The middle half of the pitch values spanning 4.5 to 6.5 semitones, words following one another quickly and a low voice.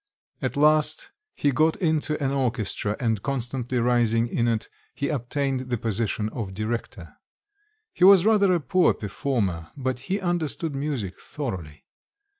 No: average, 5.0 semitones; average, 140 wpm; low, 130 Hz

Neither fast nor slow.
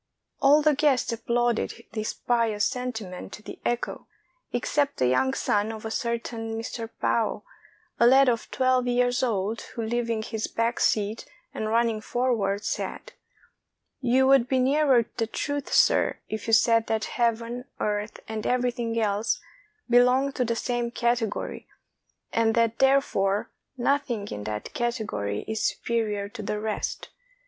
Yes: average, 150 wpm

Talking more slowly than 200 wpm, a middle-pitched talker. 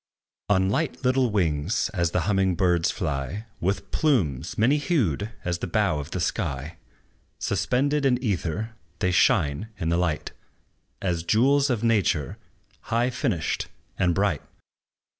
No: average, 140 wpm; very low, 95 Hz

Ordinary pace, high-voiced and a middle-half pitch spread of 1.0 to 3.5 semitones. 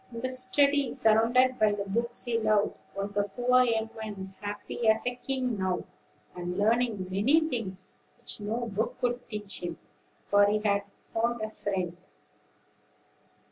Yes: average, 155 wpm; high, 220 Hz; average, 3.2 semitones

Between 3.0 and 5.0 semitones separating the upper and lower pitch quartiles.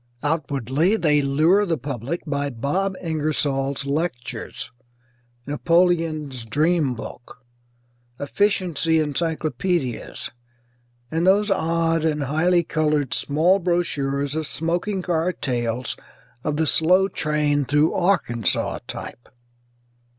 Yes: average, 3.7 semitones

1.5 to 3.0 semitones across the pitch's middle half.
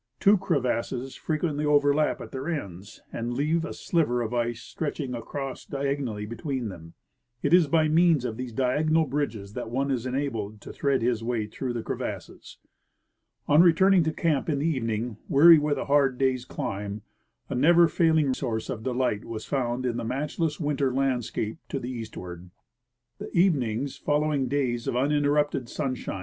No: average, 4.0 semitones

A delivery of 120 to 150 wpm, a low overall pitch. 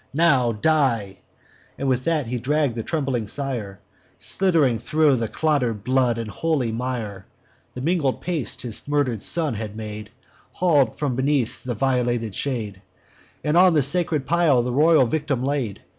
Yes: average, 145 wpm; low, 130 Hz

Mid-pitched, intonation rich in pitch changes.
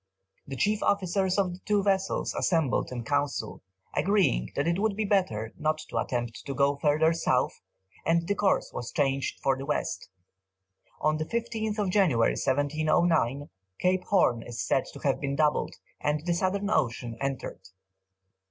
Yes: medium, 155 Hz; wide, 5.9 semitones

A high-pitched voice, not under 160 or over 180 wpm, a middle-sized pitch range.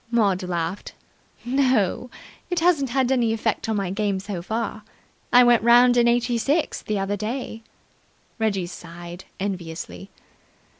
No: high, 220 Hz; average, 140 wpm; average, 4.1 semitones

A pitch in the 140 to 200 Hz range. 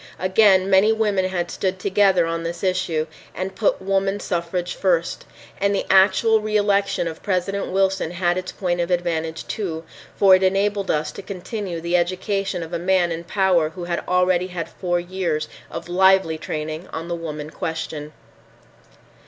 Yes: medium, 185 Hz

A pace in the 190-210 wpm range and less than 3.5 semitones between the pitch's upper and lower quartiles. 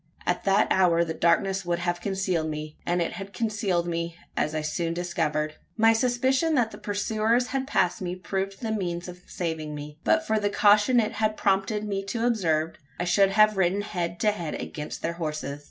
No: average, 200 wpm; average, 4.0 semitones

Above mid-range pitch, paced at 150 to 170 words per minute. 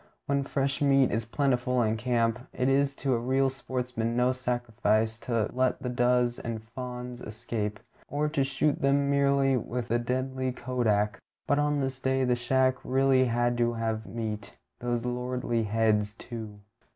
No: low, 125 Hz; average, 165 wpm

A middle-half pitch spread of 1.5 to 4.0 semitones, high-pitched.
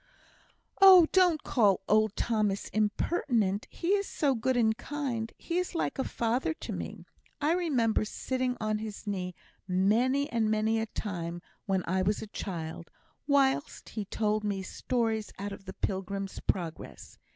No: average, 4.8 semitones; high, 220 Hz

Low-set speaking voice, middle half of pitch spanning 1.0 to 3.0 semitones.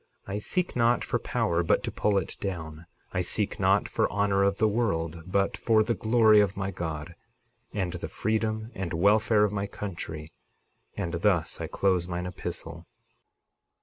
No: low, 100 Hz; average, 3.7 semitones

